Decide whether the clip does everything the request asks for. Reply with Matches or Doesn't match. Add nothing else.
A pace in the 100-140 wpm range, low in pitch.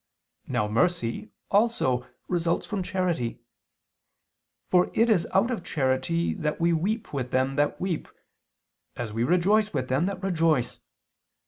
Doesn't match